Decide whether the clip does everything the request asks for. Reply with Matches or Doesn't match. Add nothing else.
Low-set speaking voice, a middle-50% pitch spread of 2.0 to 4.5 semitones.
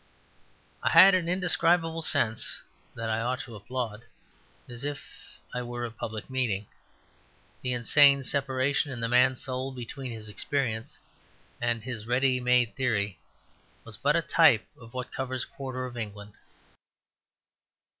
Matches